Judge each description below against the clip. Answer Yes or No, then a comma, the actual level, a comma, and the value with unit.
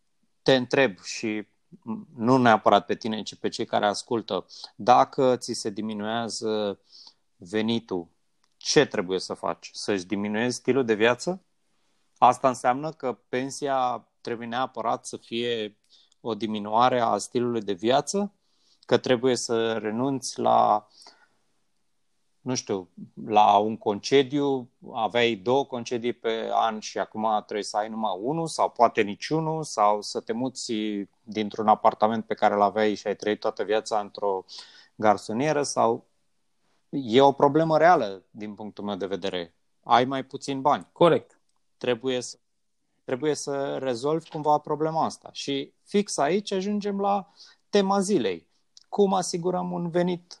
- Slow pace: No, average, 140 wpm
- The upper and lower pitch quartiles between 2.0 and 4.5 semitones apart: No, wide, 5.4 semitones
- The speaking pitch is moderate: No, low, 120 Hz